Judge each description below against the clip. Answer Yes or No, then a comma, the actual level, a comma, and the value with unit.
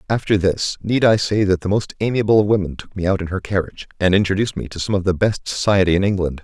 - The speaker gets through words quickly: Yes, fast, 260 wpm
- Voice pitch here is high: No, very low, 95 Hz